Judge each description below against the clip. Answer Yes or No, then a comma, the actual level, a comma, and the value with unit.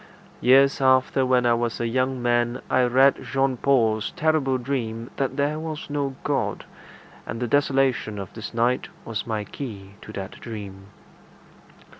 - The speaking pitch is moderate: No, low, 125 Hz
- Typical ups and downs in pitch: Yes, average, 3.0 semitones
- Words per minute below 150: No, average, 155 wpm